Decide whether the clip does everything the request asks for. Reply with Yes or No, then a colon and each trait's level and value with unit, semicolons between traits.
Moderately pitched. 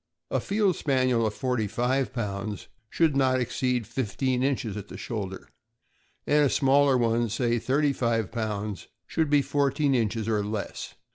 No: low, 125 Hz